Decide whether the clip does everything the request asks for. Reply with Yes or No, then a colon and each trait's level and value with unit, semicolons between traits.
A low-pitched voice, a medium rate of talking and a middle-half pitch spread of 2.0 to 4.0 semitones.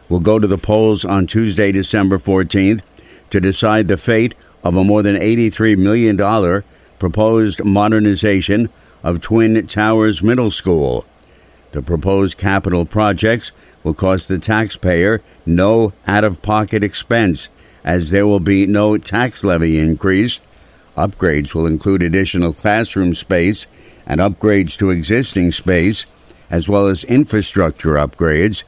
No: low, 100 Hz; slow, 130 wpm; average, 3.2 semitones